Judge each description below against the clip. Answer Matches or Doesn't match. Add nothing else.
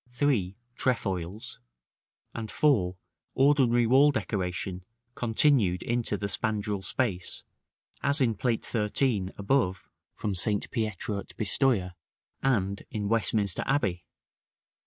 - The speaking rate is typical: Doesn't match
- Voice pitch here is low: Matches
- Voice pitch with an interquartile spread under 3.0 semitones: Doesn't match